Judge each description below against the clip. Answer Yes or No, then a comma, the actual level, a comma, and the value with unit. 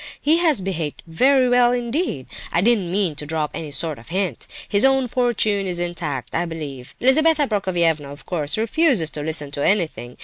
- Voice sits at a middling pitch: Yes, medium, 180 Hz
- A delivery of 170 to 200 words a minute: Yes, average, 180 wpm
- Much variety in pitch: Yes, wide, 7.8 semitones